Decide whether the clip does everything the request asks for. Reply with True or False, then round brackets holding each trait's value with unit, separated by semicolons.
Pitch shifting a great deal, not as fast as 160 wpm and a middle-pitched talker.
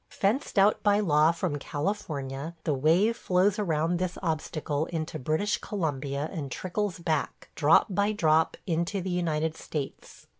False (4.2 semitones; 145 wpm; 165 Hz)